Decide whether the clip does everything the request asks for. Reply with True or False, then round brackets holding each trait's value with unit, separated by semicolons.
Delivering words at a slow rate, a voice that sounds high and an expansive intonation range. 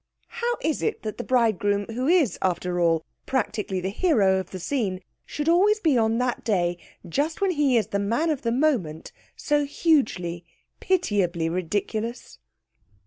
False (160 wpm; 225 Hz; 7.9 semitones)